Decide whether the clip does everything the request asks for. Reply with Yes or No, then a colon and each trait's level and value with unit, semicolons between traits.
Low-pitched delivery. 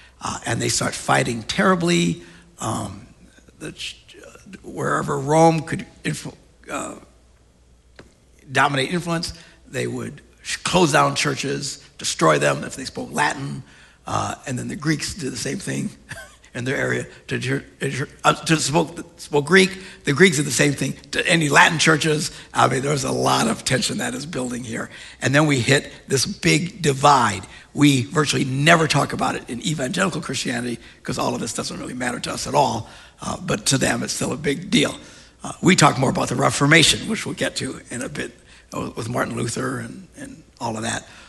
No: medium, 145 Hz